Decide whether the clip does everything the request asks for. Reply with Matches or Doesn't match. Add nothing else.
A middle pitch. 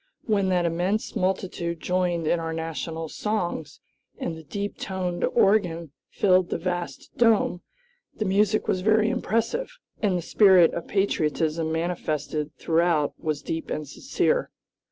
Matches